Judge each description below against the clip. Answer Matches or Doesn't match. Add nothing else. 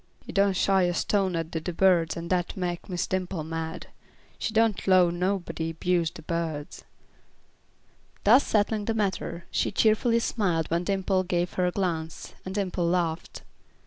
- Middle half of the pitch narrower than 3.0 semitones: Matches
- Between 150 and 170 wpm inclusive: Matches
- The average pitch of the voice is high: Doesn't match